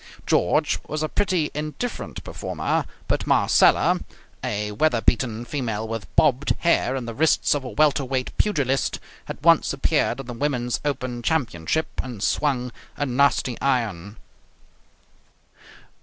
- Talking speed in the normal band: No, slow, 130 wpm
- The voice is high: No, low, 130 Hz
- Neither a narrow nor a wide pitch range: Yes, average, 4.3 semitones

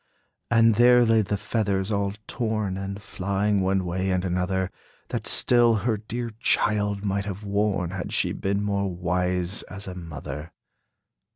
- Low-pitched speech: Yes, low, 100 Hz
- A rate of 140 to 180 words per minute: Yes, average, 155 wpm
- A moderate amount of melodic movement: No, narrow, 2.3 semitones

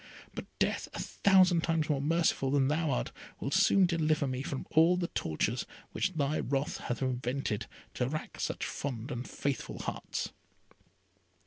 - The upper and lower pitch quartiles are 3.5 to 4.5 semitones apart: Yes, average, 3.9 semitones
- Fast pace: No, average, 155 wpm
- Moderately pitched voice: Yes, medium, 145 Hz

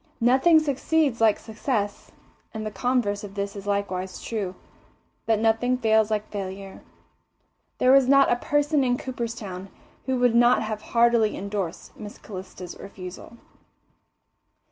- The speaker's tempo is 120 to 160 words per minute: Yes, slow, 135 wpm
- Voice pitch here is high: Yes, high, 220 Hz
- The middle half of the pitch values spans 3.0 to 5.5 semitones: Yes, average, 3.7 semitones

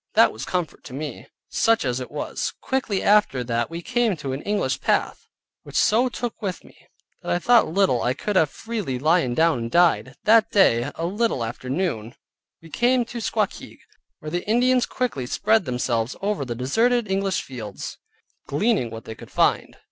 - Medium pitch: Yes, medium, 175 Hz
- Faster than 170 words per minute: Yes, average, 180 wpm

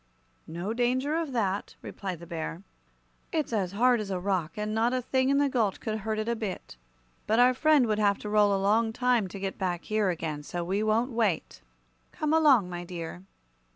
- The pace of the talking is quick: Yes, fast, 210 wpm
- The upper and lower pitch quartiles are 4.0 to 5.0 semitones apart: Yes, average, 4.6 semitones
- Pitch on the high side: Yes, high, 215 Hz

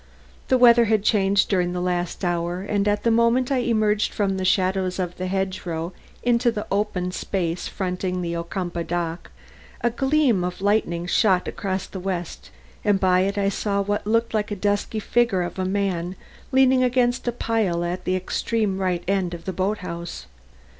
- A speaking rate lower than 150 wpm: No, average, 180 wpm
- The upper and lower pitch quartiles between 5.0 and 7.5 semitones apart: No, average, 3.2 semitones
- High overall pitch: Yes, high, 195 Hz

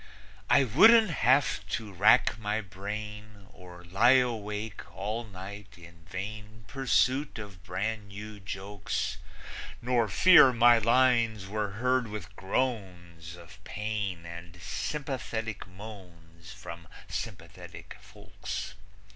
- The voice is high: No, low, 105 Hz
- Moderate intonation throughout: Yes, average, 3.5 semitones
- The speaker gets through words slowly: Yes, slow, 110 wpm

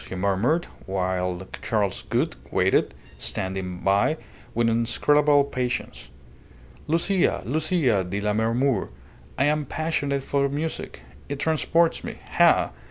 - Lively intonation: Yes, wide, 7.3 semitones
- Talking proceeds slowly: Yes, slow, 110 wpm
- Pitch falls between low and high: No, low, 125 Hz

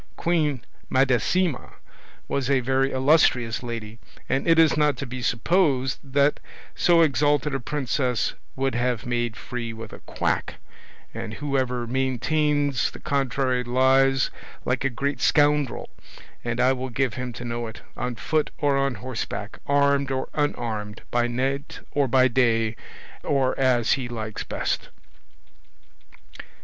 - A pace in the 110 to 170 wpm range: Yes, average, 140 wpm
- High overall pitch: No, low, 130 Hz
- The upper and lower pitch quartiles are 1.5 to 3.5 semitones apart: Yes, average, 2.7 semitones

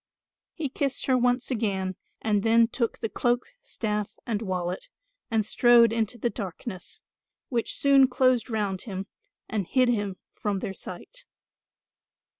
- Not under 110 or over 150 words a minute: Yes, average, 140 wpm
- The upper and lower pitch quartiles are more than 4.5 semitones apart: No, average, 3.6 semitones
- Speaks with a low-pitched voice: No, high, 225 Hz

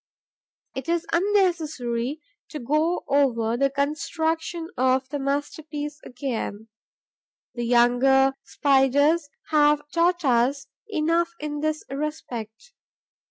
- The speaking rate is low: Yes, slow, 100 wpm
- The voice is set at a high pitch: Yes, very high, 290 Hz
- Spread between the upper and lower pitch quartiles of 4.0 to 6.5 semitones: No, average, 3.6 semitones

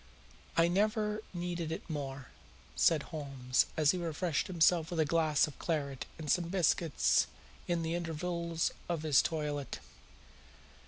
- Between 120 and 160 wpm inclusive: Yes, average, 140 wpm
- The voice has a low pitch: No, medium, 165 Hz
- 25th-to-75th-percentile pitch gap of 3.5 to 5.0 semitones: No, narrow, 2.6 semitones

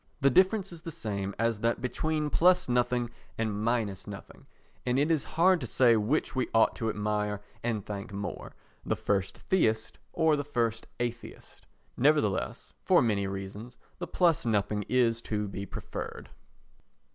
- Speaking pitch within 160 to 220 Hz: No, low, 115 Hz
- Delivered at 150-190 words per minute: Yes, average, 155 wpm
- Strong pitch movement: Yes, wide, 5.7 semitones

